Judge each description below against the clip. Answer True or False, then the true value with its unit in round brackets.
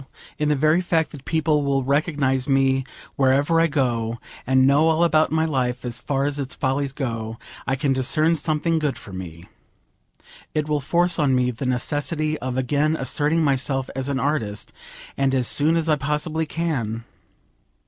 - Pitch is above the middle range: False (140 Hz)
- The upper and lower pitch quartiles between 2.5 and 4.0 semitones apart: True (2.9 semitones)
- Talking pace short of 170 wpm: False (180 wpm)